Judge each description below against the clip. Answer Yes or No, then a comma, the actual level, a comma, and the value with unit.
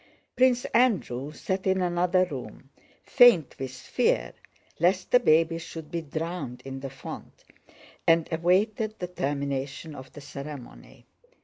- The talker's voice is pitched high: No, medium, 165 Hz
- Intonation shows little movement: No, average, 5.0 semitones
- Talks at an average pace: No, slow, 130 wpm